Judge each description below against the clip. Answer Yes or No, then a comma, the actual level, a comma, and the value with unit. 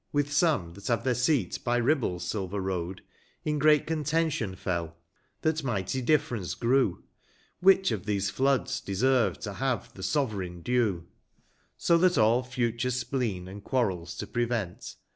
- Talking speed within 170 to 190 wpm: No, average, 150 wpm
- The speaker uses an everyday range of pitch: No, wide, 6.2 semitones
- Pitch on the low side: Yes, low, 120 Hz